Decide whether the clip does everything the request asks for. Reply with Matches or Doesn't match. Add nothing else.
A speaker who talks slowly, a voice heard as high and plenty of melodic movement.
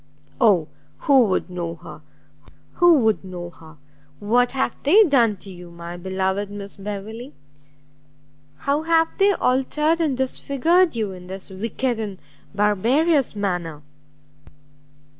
Matches